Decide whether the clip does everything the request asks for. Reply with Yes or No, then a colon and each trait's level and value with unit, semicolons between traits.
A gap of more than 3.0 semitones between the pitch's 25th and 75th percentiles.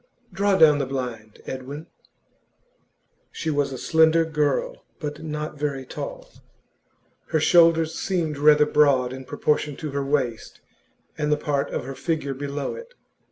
No: average, 2.7 semitones